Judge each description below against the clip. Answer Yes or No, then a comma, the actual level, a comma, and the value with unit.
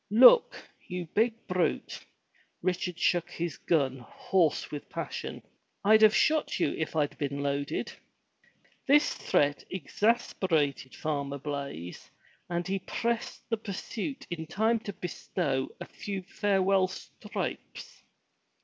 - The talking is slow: Yes, slow, 120 wpm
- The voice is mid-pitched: Yes, medium, 180 Hz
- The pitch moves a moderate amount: No, wide, 6.3 semitones